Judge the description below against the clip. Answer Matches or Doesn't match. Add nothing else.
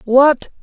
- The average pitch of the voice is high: Matches